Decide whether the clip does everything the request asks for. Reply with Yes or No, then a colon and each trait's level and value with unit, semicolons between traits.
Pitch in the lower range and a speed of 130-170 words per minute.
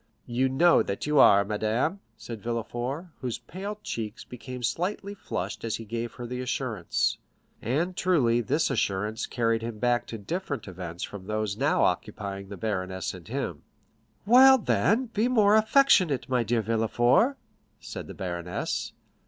Yes: low, 120 Hz; average, 155 wpm